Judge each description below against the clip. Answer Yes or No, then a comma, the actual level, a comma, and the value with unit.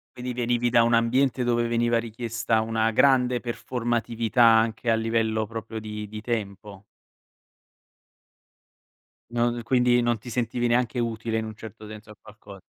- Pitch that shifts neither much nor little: No, narrow, 1.5 semitones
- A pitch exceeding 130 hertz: No, low, 115 Hz